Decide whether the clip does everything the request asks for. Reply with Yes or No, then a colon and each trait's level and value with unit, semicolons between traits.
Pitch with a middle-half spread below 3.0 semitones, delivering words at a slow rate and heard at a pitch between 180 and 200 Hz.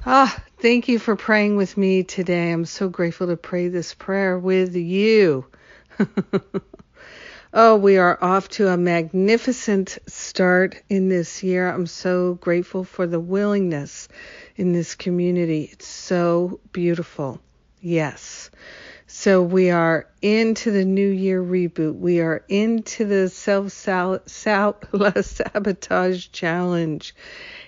Yes: narrow, 2.5 semitones; slow, 125 wpm; medium, 185 Hz